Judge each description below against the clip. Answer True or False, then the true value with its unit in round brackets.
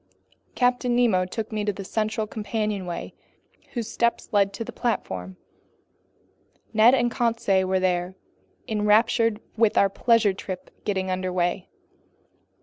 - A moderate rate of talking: False (130 wpm)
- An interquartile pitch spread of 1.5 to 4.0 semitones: True (3.5 semitones)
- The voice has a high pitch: True (210 Hz)